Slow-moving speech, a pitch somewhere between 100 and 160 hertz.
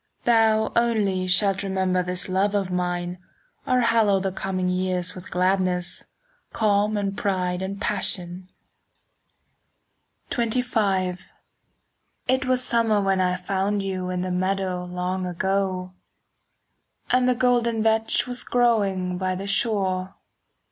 No: slow, 125 wpm; high, 195 Hz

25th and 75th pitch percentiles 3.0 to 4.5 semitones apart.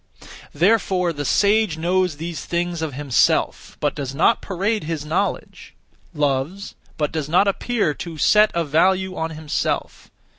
Yes: average, 4.0 semitones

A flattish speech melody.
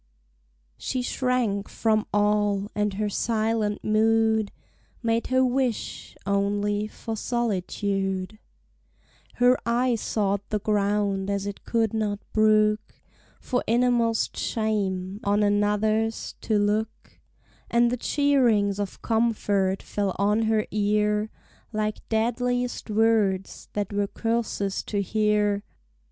Yes: narrow, 1.9 semitones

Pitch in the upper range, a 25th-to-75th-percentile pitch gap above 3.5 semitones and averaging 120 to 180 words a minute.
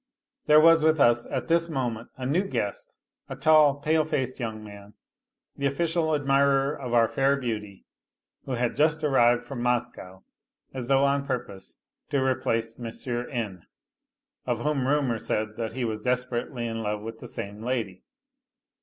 No: low, 125 Hz; average, 3.9 semitones; average, 160 wpm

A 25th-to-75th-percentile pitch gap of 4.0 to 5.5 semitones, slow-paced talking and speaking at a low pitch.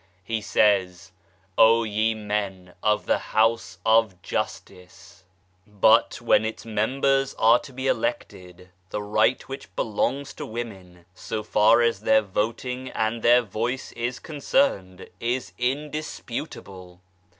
Yes: average, 4.5 semitones; slow, 130 wpm; low, 110 Hz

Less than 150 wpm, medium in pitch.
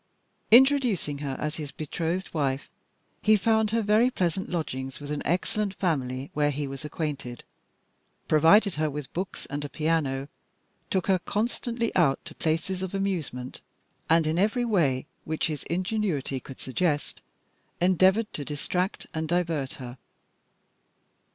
Yes: average, 140 wpm; medium, 160 Hz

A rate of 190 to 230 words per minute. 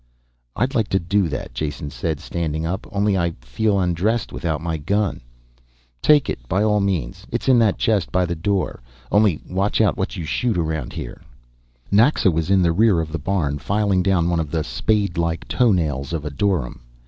Yes: average, 195 wpm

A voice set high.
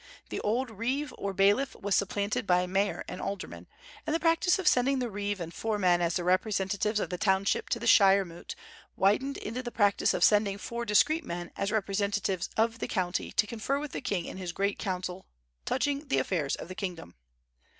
Yes: high, 200 Hz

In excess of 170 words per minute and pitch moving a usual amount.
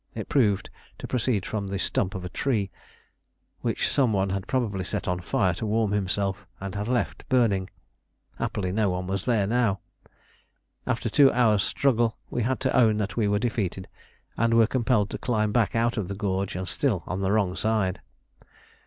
Yes: average, 190 wpm; average, 3.3 semitones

